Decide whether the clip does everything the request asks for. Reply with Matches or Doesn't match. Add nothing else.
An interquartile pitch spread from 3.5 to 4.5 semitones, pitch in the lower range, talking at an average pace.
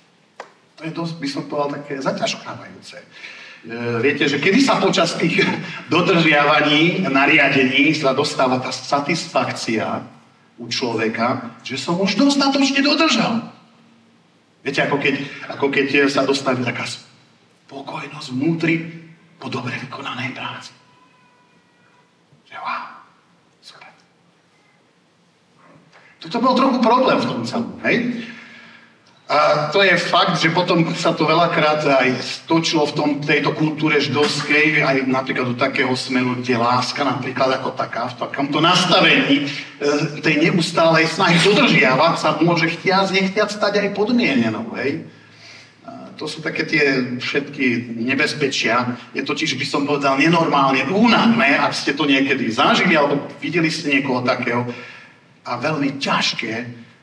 Doesn't match